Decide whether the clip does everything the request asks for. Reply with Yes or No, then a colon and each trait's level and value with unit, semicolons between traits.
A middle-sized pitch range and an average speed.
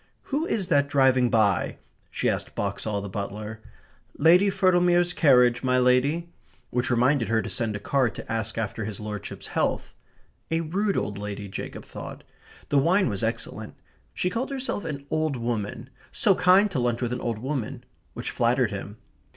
No: wide, 7.1 semitones; average, 170 wpm